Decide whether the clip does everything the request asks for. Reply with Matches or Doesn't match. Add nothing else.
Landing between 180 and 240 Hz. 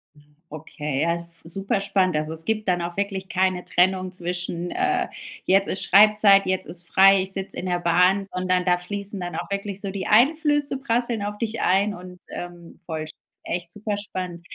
Matches